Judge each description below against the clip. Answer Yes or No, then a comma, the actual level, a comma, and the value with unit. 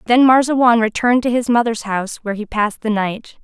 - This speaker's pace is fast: Yes, fast, 210 wpm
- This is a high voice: Yes, high, 230 Hz